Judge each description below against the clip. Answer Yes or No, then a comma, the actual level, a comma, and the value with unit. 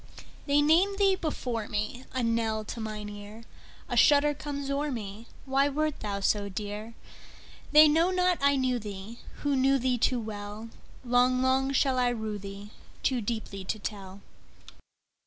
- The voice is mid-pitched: No, high, 245 Hz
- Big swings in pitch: No, average, 5.0 semitones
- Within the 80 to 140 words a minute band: Yes, slow, 135 wpm